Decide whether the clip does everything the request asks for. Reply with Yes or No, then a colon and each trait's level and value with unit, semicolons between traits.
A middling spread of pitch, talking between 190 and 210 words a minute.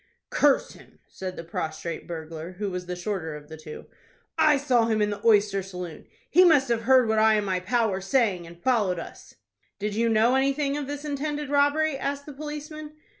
No: wide, 7.6 semitones; average, 200 wpm